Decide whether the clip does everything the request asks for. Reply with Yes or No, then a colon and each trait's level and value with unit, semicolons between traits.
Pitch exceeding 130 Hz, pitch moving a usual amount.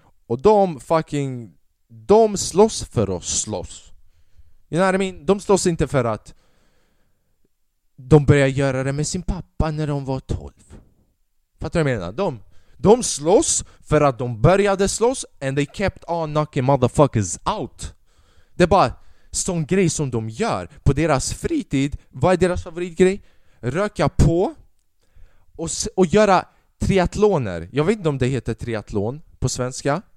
No: medium, 140 Hz; wide, 8.9 semitones